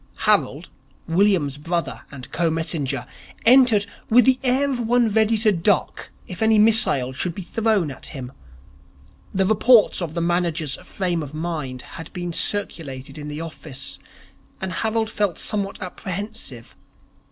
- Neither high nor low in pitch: Yes, medium, 180 Hz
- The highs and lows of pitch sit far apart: Yes, wide, 5.8 semitones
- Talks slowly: No, average, 145 wpm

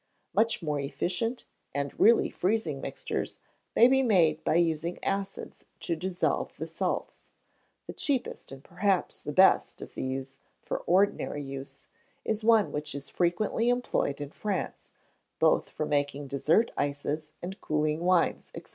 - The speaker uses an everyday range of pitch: No, wide, 6.2 semitones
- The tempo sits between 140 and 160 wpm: Yes, average, 145 wpm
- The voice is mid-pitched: Yes, medium, 170 Hz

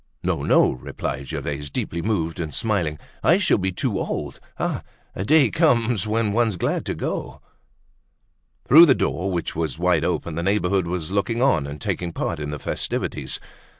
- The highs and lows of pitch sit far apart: Yes, wide, 5.8 semitones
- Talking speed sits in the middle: Yes, average, 175 wpm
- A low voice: Yes, very low, 95 Hz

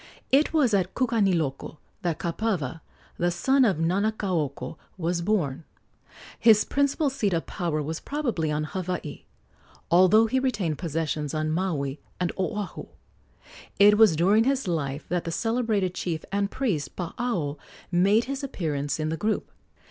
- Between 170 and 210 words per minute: No, average, 140 wpm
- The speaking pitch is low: No, medium, 180 Hz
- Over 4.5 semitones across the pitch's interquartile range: Yes, wide, 5.5 semitones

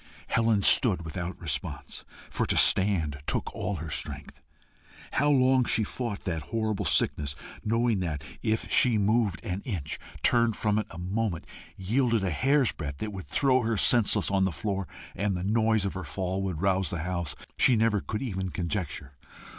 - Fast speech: No, average, 175 wpm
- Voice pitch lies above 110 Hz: No, low, 100 Hz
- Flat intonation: No, average, 4.1 semitones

